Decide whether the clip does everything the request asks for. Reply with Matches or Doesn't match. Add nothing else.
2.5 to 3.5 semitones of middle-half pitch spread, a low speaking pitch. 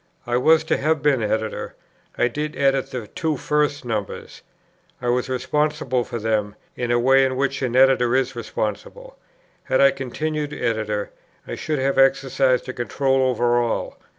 Matches